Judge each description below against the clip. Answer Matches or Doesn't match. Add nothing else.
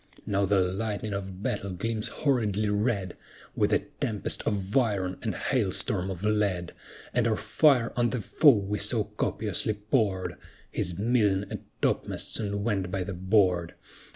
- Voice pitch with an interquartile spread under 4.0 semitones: Matches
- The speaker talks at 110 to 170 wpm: Matches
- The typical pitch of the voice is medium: Doesn't match